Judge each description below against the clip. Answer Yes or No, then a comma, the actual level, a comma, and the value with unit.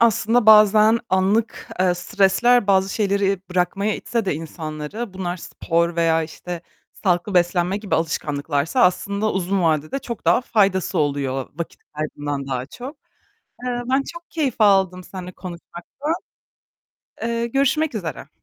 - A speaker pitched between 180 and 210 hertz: Yes, high, 190 Hz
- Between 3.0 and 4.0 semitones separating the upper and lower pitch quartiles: No, average, 4.5 semitones